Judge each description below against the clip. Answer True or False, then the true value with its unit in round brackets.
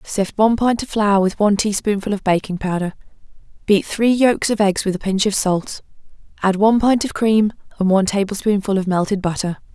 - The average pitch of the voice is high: True (200 Hz)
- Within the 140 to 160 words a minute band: False (195 wpm)